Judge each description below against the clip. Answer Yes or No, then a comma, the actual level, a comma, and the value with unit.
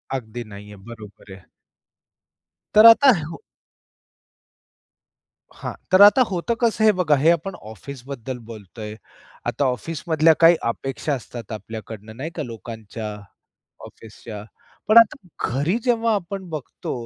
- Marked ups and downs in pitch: Yes, wide, 8.6 semitones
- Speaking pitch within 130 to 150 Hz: Yes, medium, 140 Hz